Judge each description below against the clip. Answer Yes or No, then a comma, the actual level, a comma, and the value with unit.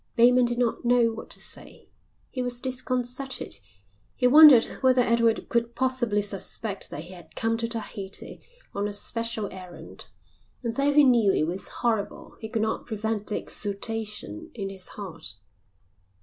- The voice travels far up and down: No, average, 3.2 semitones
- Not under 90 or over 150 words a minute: No, average, 160 wpm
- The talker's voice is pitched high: Yes, high, 230 Hz